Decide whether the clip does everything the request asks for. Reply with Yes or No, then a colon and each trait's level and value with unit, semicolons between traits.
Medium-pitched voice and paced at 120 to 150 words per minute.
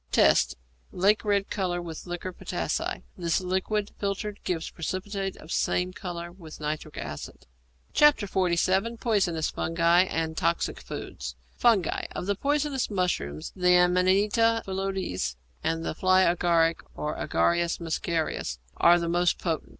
Yes: medium, 180 Hz; slow, 135 wpm